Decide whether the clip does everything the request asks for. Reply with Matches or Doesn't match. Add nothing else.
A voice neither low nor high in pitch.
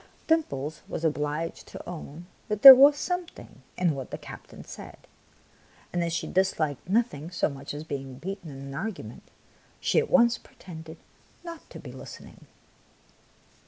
Matches